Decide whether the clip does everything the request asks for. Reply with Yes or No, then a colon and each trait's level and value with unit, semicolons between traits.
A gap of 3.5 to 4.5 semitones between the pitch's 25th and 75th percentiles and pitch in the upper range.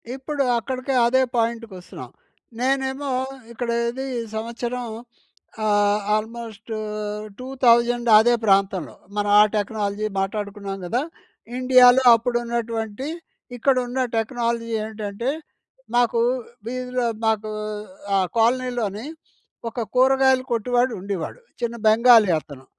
No: average, 2.8 semitones; high, 235 Hz